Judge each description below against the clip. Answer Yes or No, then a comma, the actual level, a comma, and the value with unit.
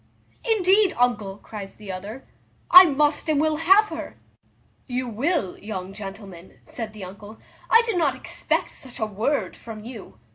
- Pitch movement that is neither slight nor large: No, wide, 7.3 semitones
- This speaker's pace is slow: No, average, 155 wpm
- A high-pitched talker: Yes, high, 235 Hz